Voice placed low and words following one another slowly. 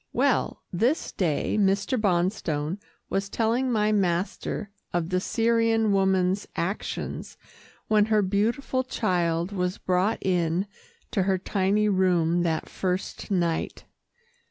No: high, 190 Hz; slow, 115 wpm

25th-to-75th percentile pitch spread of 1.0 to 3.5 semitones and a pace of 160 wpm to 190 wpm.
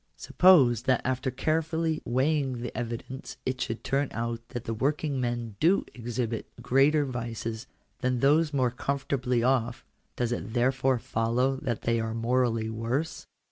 No: average, 2.7 semitones; average, 145 wpm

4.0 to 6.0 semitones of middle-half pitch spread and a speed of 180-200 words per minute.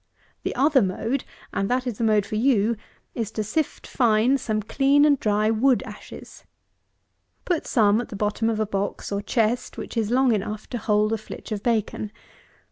No: average, 3.0 semitones; average, 190 wpm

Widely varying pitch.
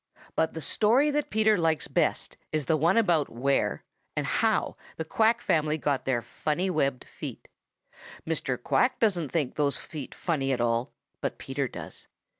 Yes: wide, 5.7 semitones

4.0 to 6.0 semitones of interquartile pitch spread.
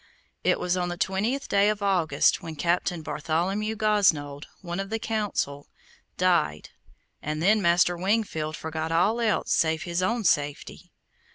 Yes: average, 4.5 semitones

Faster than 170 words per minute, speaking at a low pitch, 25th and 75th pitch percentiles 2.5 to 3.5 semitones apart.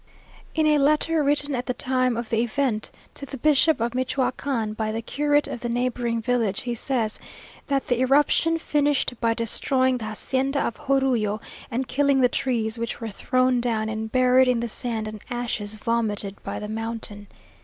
No: average, 180 wpm; high, 245 Hz; average, 3.2 semitones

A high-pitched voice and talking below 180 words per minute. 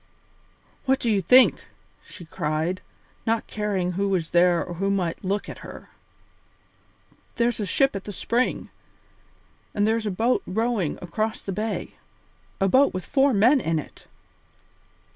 Yes: high, 200 Hz; average, 150 wpm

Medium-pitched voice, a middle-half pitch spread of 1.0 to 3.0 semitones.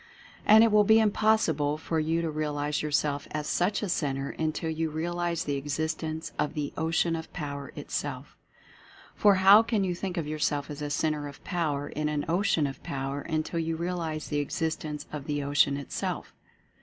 Yes: medium, 155 Hz; average, 2.7 semitones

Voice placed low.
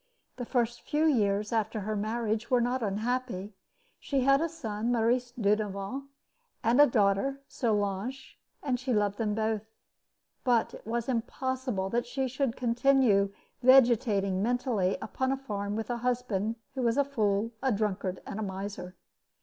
No: high, 230 Hz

